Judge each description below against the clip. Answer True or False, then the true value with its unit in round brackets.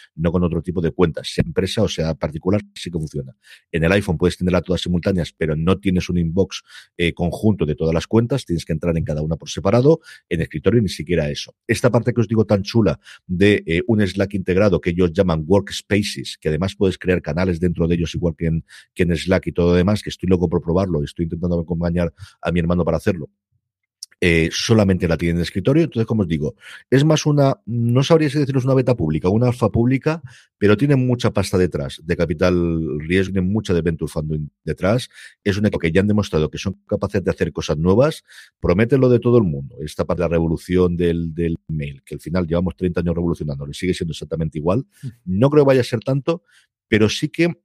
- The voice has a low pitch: True (90 Hz)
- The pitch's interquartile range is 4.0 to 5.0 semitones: True (4.7 semitones)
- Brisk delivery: True (225 wpm)